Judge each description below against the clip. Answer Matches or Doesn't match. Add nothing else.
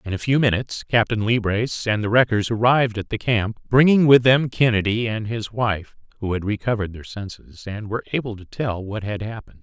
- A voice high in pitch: Doesn't match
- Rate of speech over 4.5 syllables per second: Matches